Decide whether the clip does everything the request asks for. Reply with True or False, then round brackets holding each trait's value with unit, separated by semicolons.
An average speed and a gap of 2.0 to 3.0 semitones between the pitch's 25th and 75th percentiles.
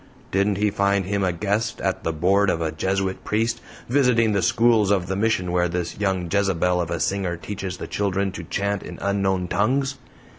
True (195 wpm; 2.4 semitones)